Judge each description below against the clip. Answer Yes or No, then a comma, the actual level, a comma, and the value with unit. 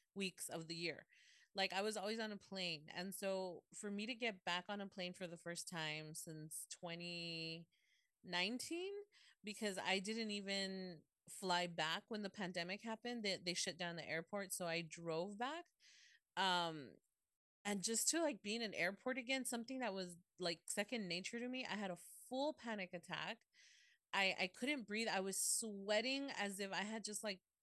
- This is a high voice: Yes, high, 195 Hz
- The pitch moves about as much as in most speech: Yes, average, 4.3 semitones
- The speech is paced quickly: No, average, 185 wpm